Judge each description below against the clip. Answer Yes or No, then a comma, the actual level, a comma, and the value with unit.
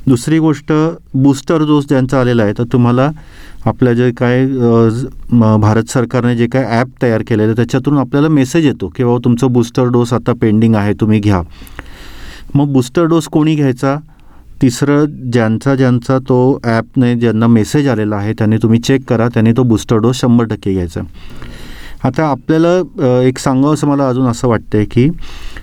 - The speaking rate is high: Yes, fast, 165 wpm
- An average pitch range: Yes, average, 3.3 semitones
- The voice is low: Yes, low, 125 Hz